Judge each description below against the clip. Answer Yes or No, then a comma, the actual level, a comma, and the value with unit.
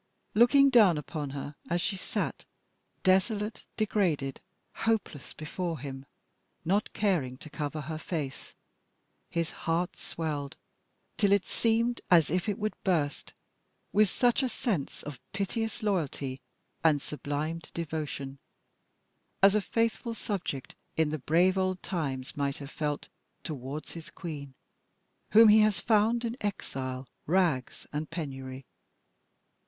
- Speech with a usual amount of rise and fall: No, wide, 6.2 semitones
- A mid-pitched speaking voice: Yes, medium, 165 Hz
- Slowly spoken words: Yes, slow, 125 wpm